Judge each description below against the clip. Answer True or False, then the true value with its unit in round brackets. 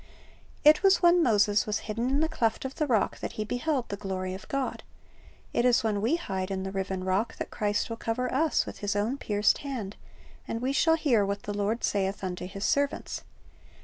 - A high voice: True (220 Hz)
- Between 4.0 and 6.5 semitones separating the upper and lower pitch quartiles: True (5.2 semitones)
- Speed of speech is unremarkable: False (215 wpm)